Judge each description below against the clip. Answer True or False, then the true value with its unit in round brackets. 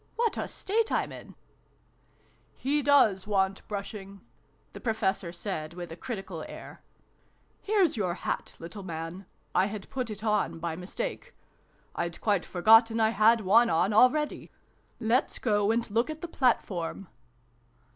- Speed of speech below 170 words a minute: True (155 wpm)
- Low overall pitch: False (210 Hz)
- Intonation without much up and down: False (4.5 semitones)